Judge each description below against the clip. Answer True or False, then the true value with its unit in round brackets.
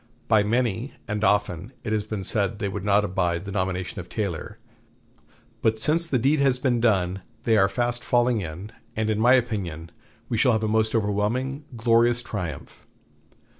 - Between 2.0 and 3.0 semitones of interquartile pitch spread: False (3.5 semitones)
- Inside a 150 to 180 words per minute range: True (175 wpm)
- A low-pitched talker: True (110 Hz)